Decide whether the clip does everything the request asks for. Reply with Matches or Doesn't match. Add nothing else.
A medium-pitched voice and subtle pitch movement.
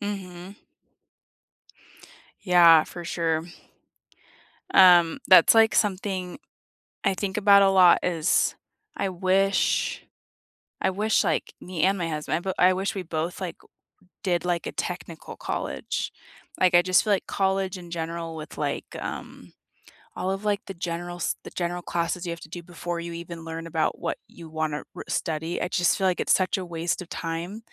Matches